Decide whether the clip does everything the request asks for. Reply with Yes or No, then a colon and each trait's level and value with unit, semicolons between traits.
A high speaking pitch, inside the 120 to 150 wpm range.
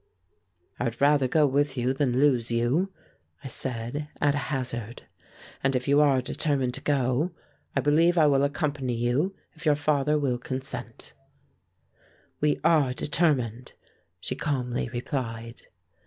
No: low, 135 Hz; average, 140 wpm